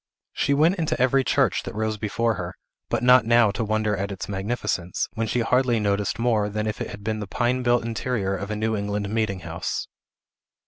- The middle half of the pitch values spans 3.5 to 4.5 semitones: No, average, 2.9 semitones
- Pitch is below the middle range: Yes, low, 110 Hz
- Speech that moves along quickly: Yes, fast, 210 wpm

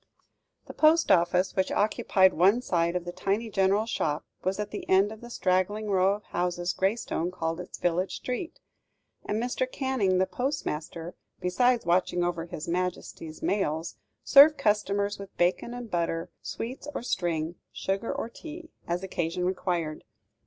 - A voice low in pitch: No, high, 190 Hz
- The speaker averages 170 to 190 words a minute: No, average, 155 wpm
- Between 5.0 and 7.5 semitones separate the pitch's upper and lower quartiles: No, average, 3.9 semitones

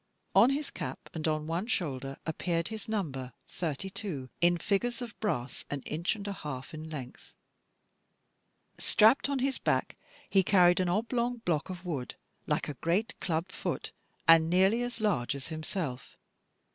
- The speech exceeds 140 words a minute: Yes, average, 160 wpm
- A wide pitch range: Yes, wide, 5.7 semitones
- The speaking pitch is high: No, medium, 175 Hz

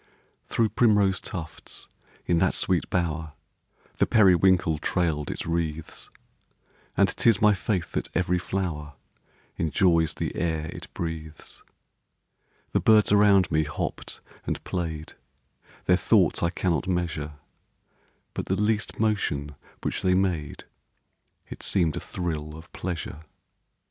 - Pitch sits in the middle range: No, very low, 85 Hz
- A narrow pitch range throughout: No, average, 3.3 semitones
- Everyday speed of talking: No, slow, 125 wpm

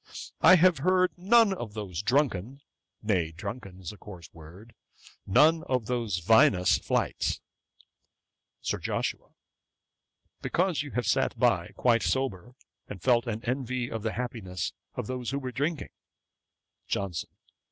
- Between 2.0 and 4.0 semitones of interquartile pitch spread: No, wide, 5.6 semitones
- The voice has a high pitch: No, low, 120 Hz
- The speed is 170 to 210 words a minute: No, slow, 135 wpm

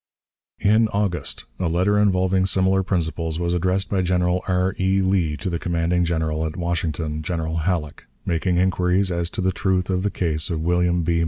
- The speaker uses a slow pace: No, average, 180 wpm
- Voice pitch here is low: Yes, very low, 90 Hz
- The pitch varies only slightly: Yes, narrow, 2.0 semitones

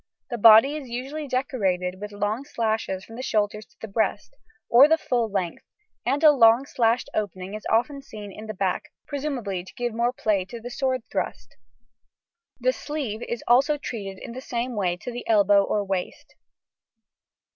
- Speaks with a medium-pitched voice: No, high, 225 Hz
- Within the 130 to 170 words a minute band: No, average, 180 wpm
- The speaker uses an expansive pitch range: No, average, 4.1 semitones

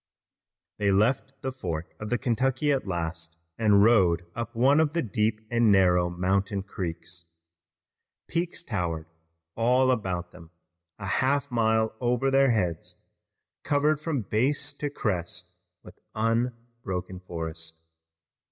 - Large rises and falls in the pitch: Yes, wide, 6.3 semitones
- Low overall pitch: Yes, low, 110 Hz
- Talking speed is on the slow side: Yes, slow, 125 wpm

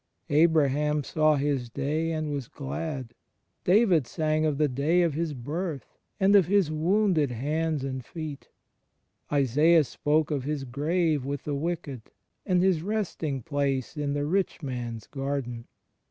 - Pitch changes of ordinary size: Yes, average, 3.0 semitones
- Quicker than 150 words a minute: No, average, 145 wpm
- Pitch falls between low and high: Yes, medium, 150 Hz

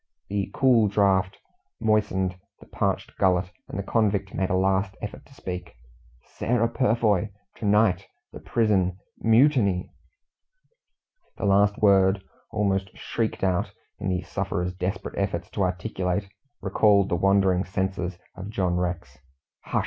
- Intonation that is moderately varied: No, narrow, 2.3 semitones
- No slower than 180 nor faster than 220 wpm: No, slow, 135 wpm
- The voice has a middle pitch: No, very low, 95 Hz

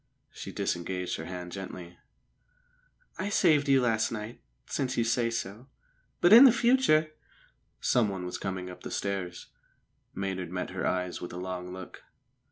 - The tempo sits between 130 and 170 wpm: Yes, average, 155 wpm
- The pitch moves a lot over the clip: Yes, wide, 5.9 semitones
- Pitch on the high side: No, very low, 95 Hz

